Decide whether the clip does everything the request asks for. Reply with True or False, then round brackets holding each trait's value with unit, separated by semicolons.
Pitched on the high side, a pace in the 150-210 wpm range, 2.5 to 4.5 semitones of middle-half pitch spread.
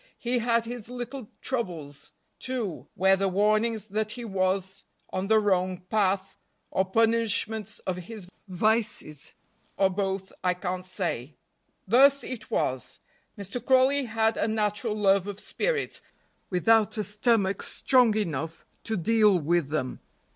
False (210 Hz; 135 wpm; 3.4 semitones)